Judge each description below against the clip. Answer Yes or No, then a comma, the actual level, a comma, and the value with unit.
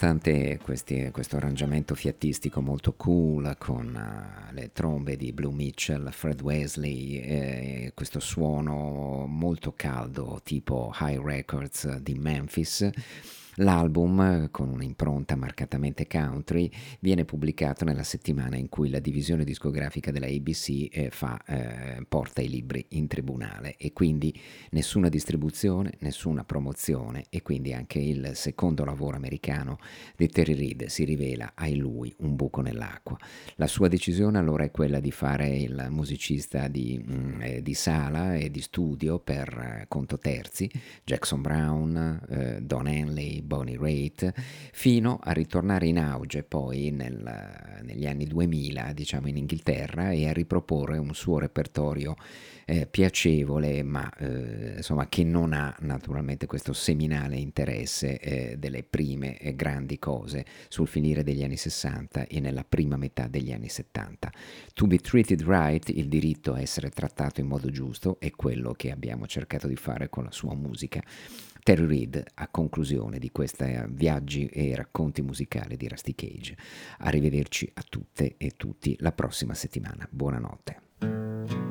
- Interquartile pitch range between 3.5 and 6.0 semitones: No, narrow, 2.6 semitones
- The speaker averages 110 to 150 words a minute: Yes, average, 140 wpm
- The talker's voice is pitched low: Yes, very low, 75 Hz